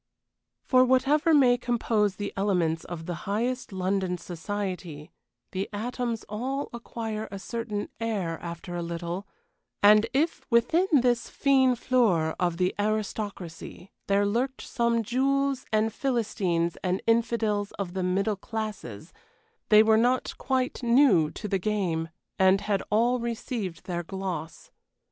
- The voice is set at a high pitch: Yes, high, 210 Hz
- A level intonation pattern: No, average, 4.6 semitones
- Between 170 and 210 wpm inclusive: No, slow, 135 wpm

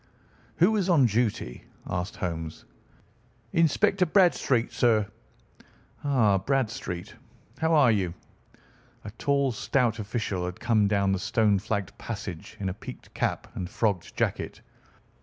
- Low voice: Yes, low, 110 Hz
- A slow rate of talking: Yes, slow, 125 wpm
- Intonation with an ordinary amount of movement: No, wide, 6.0 semitones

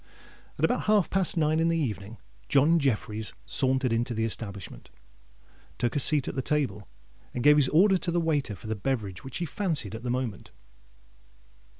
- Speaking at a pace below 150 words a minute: No, average, 185 wpm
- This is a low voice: Yes, low, 130 Hz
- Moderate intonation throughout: No, wide, 6.0 semitones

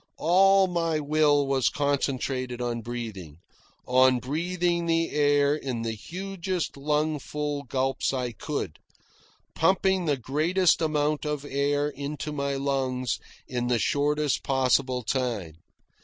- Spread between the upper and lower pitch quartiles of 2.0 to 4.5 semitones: Yes, average, 3.3 semitones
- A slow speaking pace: Yes, slow, 125 wpm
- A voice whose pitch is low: No, medium, 145 Hz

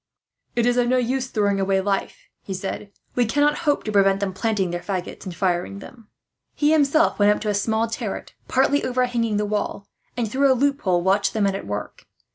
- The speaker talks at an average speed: No, fast, 210 wpm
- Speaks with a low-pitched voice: No, high, 210 Hz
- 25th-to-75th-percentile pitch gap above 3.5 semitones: Yes, average, 4.3 semitones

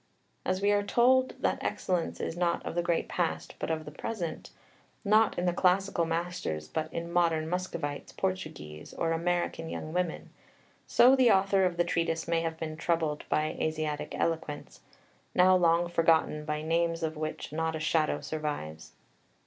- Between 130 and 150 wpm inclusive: No, average, 165 wpm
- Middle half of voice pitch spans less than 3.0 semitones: Yes, narrow, 2.4 semitones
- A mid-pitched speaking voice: Yes, medium, 165 Hz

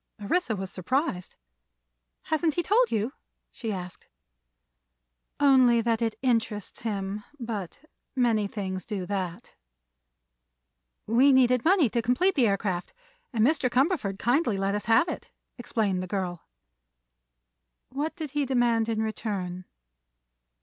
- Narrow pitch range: No, average, 4.9 semitones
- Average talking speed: No, slow, 125 wpm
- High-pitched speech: Yes, high, 230 Hz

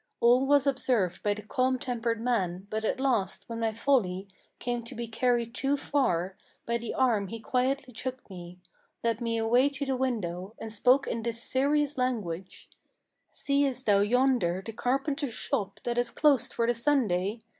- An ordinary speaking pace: Yes, average, 175 wpm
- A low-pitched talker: No, high, 235 Hz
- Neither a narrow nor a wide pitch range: Yes, average, 3.5 semitones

